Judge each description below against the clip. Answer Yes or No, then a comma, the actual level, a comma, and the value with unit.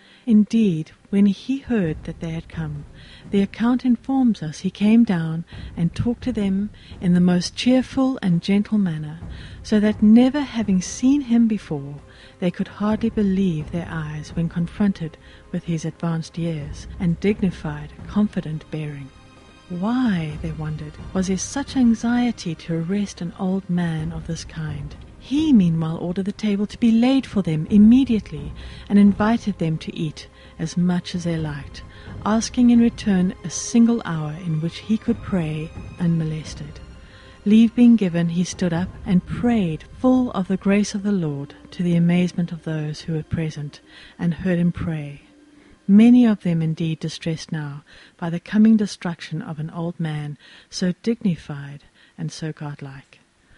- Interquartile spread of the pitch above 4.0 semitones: Yes, average, 4.9 semitones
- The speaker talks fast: No, average, 160 wpm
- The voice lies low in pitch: No, medium, 180 Hz